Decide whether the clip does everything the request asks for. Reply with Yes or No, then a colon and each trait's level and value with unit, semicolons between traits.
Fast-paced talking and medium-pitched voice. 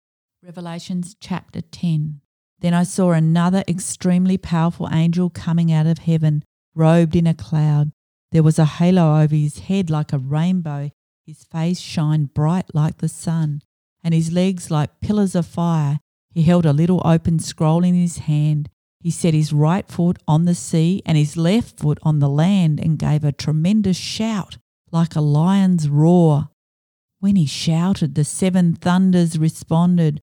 No: average, 160 wpm; medium, 165 Hz